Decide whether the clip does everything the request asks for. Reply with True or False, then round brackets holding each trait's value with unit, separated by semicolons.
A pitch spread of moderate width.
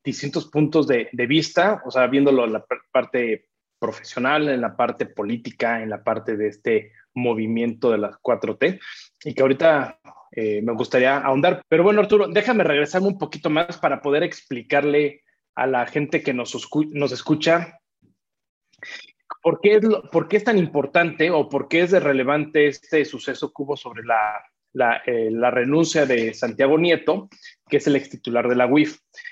True (4.7 semitones)